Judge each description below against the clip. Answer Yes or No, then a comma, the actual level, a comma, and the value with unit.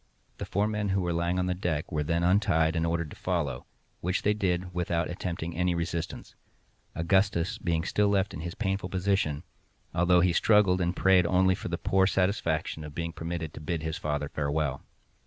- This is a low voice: Yes, very low, 85 Hz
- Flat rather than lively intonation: Yes, narrow, 2.3 semitones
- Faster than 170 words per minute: Yes, average, 190 wpm